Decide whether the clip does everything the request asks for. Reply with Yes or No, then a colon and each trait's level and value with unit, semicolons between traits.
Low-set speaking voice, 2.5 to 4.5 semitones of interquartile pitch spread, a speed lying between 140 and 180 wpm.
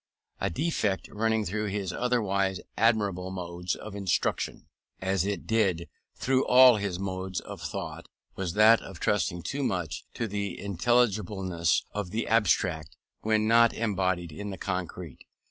Yes: low, 100 Hz; average, 3.2 semitones; average, 145 wpm